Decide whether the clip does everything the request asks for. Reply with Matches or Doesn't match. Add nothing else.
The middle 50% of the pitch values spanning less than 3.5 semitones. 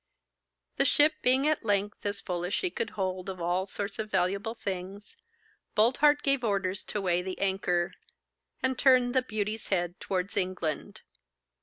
Doesn't match